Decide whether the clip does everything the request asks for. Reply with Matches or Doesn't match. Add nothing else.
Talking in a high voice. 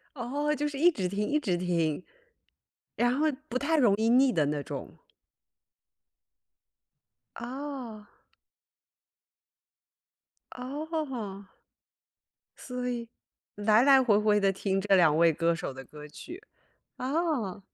Matches